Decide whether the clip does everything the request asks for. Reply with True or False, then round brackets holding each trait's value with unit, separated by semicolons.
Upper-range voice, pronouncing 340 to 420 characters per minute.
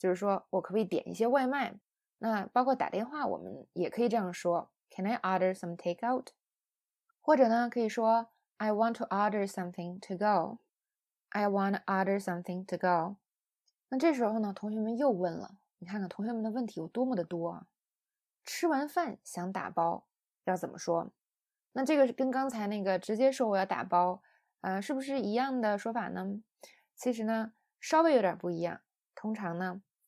True (210 Hz; 355 characters per minute)